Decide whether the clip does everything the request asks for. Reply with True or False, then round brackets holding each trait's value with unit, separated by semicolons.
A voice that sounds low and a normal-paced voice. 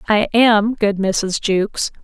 False (210 Hz; 145 wpm)